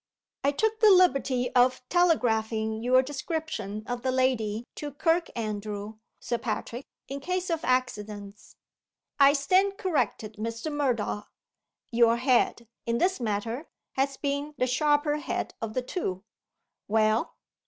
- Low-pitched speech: No, very high, 255 Hz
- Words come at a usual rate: No, slow, 130 wpm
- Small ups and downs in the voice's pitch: No, average, 4.9 semitones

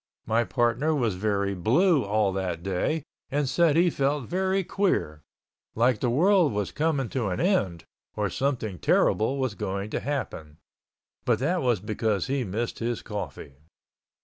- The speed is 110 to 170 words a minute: Yes, average, 155 wpm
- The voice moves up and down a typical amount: No, wide, 6.3 semitones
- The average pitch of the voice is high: No, low, 120 Hz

